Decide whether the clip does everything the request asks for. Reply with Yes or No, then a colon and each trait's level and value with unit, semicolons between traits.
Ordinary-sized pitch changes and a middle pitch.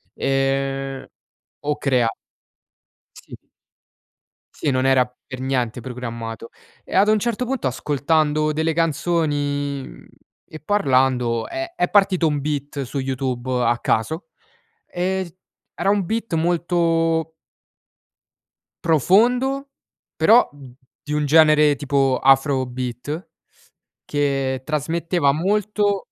Yes: average, 4.5 semitones; medium, 150 Hz